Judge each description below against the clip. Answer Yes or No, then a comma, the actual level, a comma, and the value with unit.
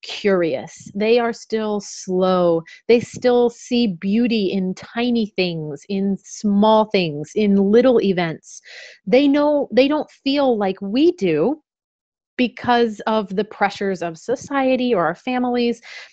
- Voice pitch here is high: Yes, high, 220 Hz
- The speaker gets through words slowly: Yes, slow, 130 wpm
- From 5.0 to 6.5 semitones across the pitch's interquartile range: No, average, 4.1 semitones